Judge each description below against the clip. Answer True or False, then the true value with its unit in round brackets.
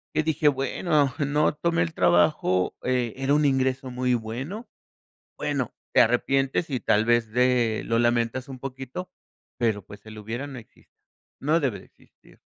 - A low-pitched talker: True (130 Hz)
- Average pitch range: True (3.7 semitones)